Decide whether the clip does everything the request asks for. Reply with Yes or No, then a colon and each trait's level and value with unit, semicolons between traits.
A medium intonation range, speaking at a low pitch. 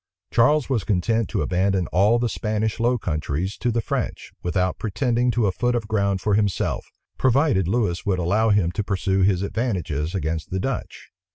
Yes: average, 4.0 semitones; low, 100 Hz